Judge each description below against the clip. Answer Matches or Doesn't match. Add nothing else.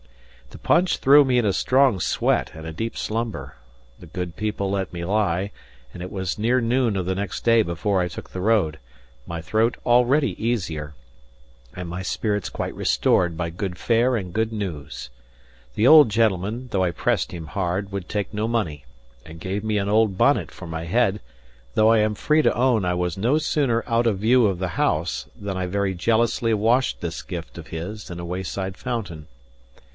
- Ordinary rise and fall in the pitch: Matches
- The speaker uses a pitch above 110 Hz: Doesn't match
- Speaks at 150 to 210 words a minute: Matches